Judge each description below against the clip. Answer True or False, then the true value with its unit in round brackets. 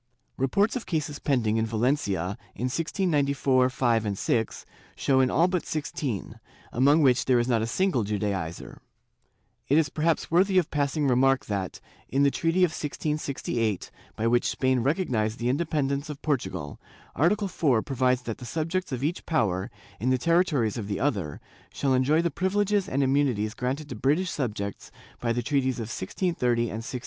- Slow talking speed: False (170 wpm)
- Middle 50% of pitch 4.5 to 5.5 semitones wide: True (5.1 semitones)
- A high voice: False (135 Hz)